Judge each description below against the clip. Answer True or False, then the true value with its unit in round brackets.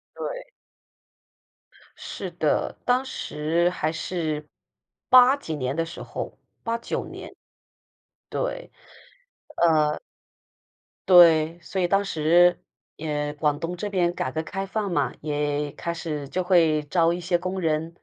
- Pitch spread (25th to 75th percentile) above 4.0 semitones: False (3.3 semitones)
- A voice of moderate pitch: True (165 Hz)